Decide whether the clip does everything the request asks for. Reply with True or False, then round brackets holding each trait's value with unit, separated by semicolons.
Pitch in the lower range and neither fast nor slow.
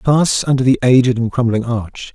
True (125 Hz; 195 wpm)